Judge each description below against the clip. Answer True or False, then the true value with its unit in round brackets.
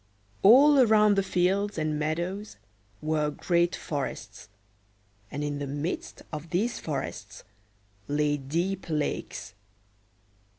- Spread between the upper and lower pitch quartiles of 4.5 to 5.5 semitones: True (4.9 semitones)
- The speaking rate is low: True (110 wpm)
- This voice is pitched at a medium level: True (160 Hz)